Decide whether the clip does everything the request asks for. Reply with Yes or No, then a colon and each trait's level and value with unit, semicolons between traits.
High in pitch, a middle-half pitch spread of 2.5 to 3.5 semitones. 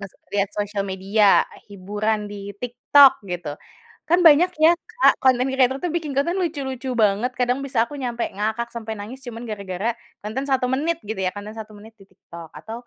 No: high, 230 Hz; average, 4.5 semitones